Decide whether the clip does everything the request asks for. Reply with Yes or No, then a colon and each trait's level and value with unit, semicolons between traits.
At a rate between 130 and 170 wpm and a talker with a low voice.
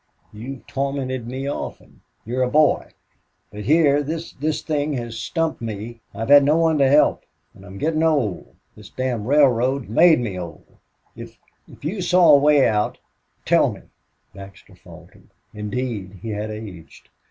Yes: average, 165 wpm; low, 130 Hz